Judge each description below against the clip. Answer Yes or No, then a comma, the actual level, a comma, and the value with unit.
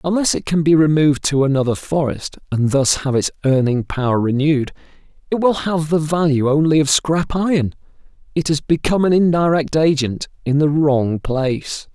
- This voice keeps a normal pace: Yes, average, 170 wpm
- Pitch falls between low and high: Yes, medium, 150 Hz